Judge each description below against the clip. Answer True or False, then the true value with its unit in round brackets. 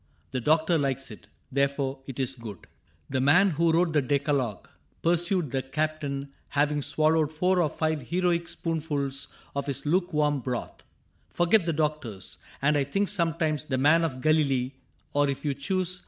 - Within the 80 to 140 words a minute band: False (165 wpm)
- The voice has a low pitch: False (150 Hz)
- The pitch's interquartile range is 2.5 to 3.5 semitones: True (3.1 semitones)